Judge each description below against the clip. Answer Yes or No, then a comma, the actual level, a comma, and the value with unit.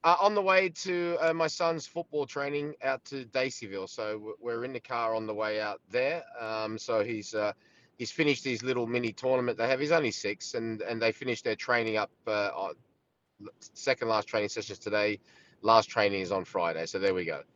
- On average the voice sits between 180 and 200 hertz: No, low, 120 Hz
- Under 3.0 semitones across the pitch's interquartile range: No, average, 5.0 semitones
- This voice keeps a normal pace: No, fast, 210 wpm